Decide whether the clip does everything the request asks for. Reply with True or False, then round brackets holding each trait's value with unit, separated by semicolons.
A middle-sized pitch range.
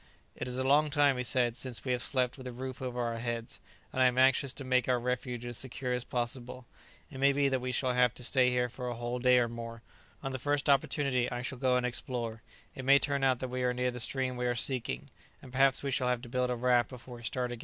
False (1.3 semitones)